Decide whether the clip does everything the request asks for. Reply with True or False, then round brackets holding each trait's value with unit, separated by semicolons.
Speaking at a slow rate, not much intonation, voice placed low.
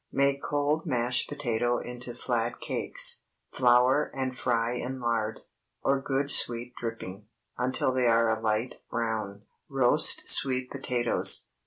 True (130 wpm; 2.3 semitones; 125 Hz)